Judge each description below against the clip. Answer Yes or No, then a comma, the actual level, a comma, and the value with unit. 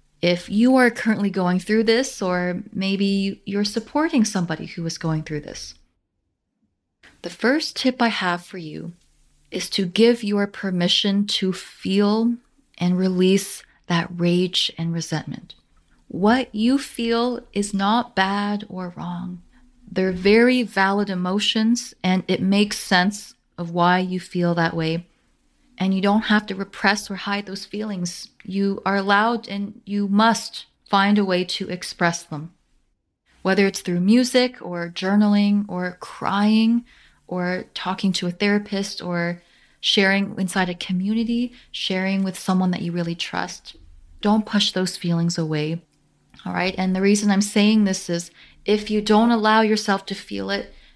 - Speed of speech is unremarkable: Yes, average, 150 wpm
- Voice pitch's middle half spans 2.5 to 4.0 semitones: Yes, average, 3.0 semitones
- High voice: Yes, high, 195 Hz